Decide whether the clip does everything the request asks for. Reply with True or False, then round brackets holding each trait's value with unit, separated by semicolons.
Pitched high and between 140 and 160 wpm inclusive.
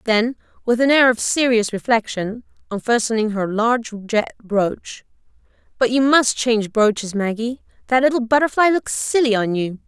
True (230 Hz; 150 wpm)